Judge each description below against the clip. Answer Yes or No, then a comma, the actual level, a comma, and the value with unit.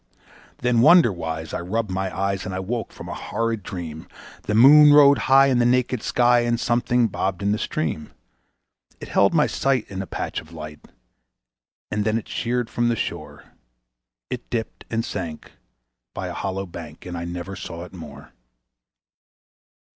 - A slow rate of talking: No, average, 175 wpm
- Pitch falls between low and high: No, low, 105 Hz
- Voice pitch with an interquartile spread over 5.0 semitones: Yes, wide, 5.5 semitones